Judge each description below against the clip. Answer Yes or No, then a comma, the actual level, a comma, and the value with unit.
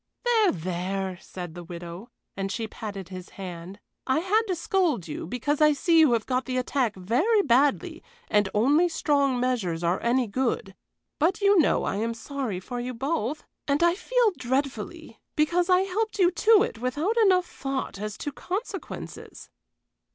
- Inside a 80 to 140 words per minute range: No, average, 165 wpm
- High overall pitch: Yes, very high, 260 Hz